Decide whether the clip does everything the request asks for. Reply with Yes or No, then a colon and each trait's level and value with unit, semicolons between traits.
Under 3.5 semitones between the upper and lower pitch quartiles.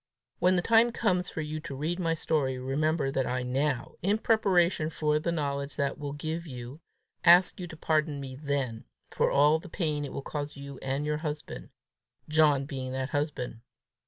Yes: average, 2.9 semitones